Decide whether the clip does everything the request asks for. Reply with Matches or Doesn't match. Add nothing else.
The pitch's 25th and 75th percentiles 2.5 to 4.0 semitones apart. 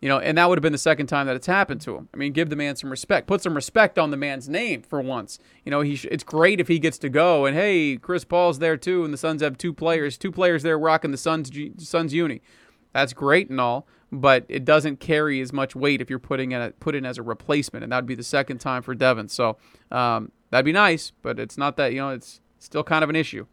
Matches